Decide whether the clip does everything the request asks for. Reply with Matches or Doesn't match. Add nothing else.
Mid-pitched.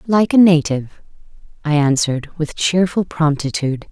Matches